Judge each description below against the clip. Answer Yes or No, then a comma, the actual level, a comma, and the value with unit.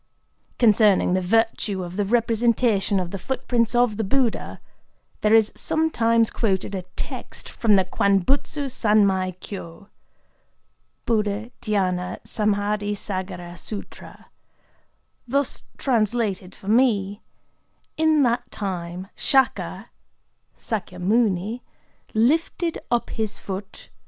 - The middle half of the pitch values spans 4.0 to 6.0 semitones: No, average, 3.6 semitones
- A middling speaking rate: No, slow, 100 wpm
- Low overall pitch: No, high, 210 Hz